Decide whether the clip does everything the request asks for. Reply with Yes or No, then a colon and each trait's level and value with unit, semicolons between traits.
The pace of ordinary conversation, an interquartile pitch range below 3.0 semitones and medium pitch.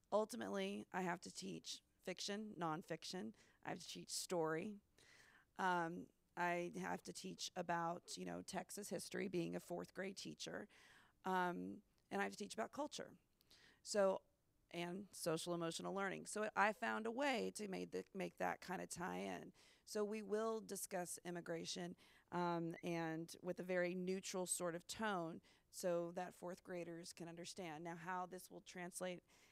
Yes: average, 160 wpm; narrow, 2.5 semitones; medium, 180 Hz